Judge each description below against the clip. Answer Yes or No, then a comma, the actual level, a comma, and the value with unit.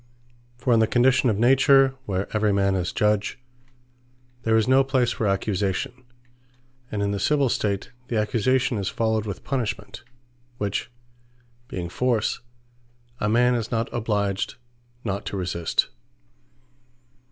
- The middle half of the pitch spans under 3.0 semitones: No, average, 3.5 semitones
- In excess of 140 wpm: No, slow, 135 wpm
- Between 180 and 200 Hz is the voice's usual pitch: No, low, 110 Hz